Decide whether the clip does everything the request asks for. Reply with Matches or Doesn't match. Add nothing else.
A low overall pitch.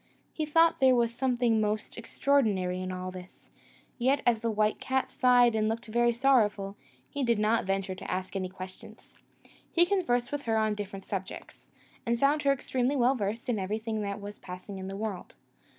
Doesn't match